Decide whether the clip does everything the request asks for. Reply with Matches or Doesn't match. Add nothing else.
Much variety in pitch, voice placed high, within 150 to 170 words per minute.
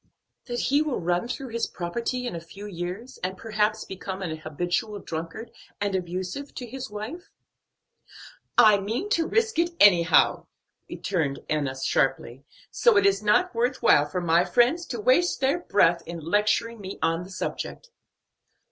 Matches